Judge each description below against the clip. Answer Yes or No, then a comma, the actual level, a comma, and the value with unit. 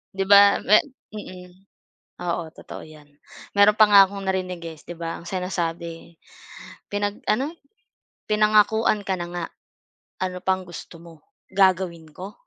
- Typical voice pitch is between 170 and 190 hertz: Yes, medium, 185 Hz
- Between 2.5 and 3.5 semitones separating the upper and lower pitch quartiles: Yes, average, 3.0 semitones